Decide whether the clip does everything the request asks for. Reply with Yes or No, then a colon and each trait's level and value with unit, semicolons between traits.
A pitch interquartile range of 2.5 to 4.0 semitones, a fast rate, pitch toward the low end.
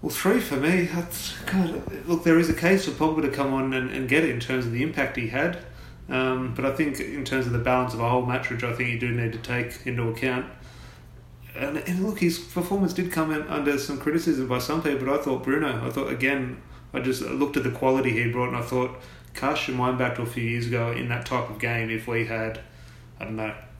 Yes: average, 3.5 semitones; fast, 255 wpm; low, 130 Hz